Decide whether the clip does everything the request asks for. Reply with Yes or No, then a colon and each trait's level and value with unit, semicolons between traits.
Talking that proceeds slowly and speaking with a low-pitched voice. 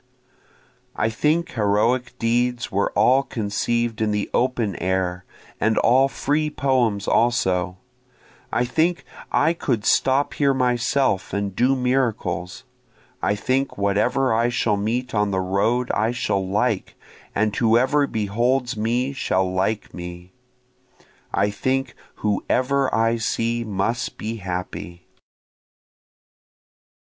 Yes: slow, 115 wpm; low, 115 Hz